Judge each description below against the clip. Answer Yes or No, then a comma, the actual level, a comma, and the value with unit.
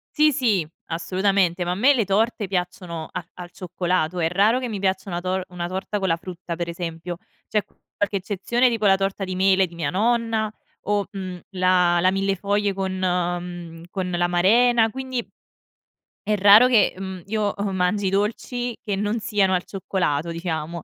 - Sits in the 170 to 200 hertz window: Yes, high, 190 Hz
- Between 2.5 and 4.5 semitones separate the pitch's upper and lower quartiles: Yes, average, 2.8 semitones